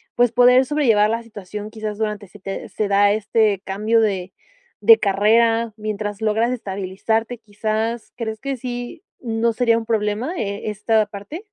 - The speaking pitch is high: Yes, high, 220 Hz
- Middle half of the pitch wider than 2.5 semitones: No, narrow, 2.0 semitones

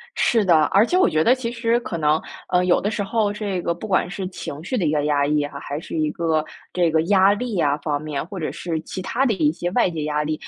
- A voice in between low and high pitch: Yes, medium, 175 Hz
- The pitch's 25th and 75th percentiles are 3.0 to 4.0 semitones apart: No, average, 5.0 semitones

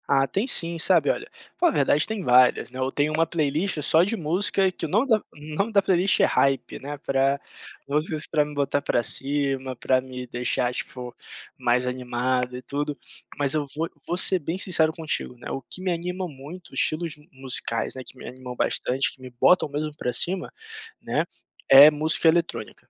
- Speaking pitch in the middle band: Yes, medium, 145 Hz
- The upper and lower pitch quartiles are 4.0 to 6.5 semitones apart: Yes, average, 4.7 semitones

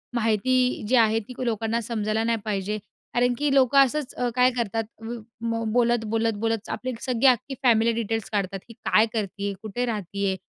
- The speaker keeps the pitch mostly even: Yes, narrow, 2.3 semitones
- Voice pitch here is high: Yes, high, 225 Hz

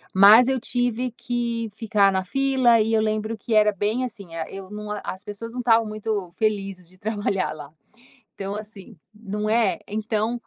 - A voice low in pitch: No, high, 215 Hz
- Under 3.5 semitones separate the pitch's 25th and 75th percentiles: Yes, narrow, 2.5 semitones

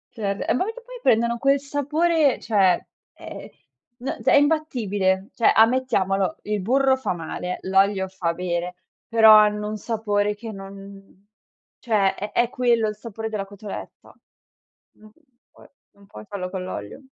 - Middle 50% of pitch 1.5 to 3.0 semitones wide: No, average, 3.8 semitones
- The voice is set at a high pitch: Yes, high, 210 Hz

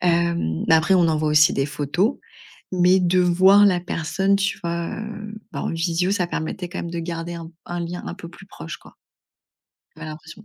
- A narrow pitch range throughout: Yes, narrow, 2.3 semitones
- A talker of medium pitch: Yes, medium, 170 Hz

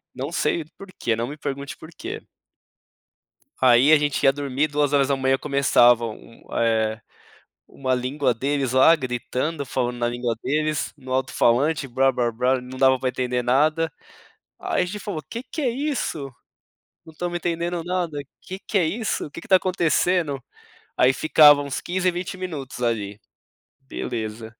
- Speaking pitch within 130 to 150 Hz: Yes, medium, 140 Hz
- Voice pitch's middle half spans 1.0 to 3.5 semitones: No, average, 4.7 semitones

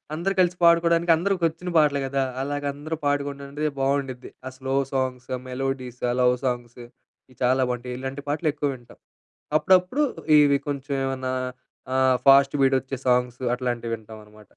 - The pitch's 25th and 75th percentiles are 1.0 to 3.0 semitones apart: Yes, average, 2.7 semitones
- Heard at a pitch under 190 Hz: Yes, low, 135 Hz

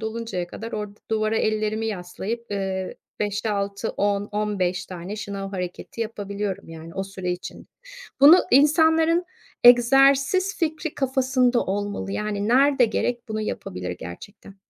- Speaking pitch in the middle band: No, high, 210 Hz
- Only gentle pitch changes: No, average, 3.9 semitones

